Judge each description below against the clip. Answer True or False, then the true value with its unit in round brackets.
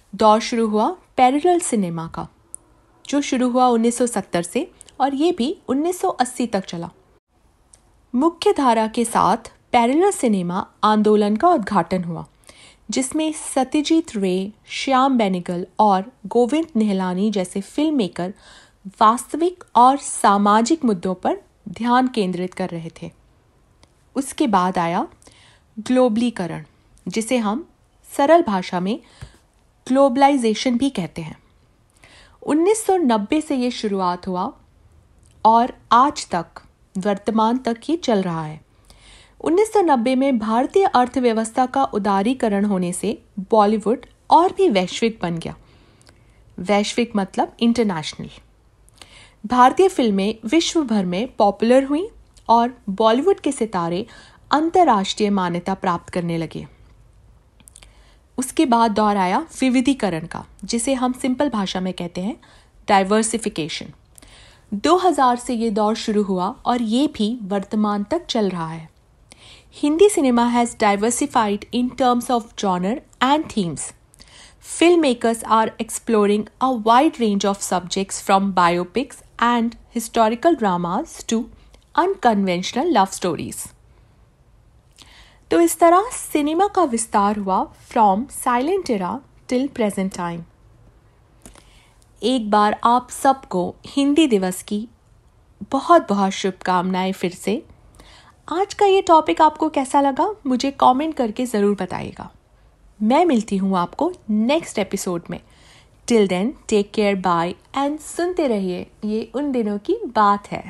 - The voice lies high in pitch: True (225 Hz)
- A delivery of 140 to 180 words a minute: False (120 wpm)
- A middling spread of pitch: False (5.7 semitones)